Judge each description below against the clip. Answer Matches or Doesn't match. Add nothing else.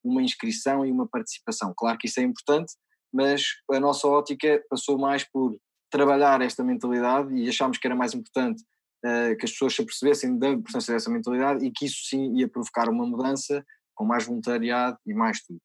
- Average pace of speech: Doesn't match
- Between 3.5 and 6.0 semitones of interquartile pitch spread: Doesn't match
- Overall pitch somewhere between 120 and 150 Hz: Matches